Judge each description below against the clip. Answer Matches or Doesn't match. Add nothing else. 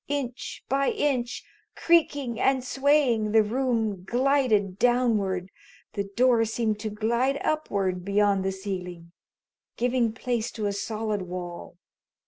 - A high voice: Matches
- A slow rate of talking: Matches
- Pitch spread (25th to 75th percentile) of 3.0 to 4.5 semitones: Matches